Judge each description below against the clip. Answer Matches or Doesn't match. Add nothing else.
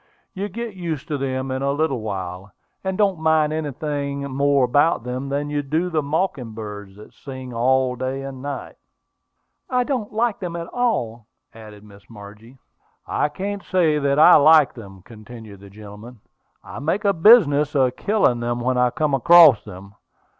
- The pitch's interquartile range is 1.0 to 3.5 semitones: Doesn't match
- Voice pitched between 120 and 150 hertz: Matches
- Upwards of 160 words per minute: Matches